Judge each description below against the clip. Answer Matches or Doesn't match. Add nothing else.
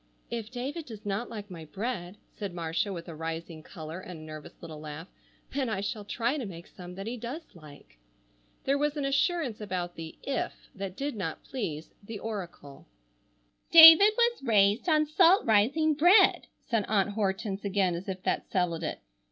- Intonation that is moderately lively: Doesn't match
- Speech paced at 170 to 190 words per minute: Matches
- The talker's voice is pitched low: Doesn't match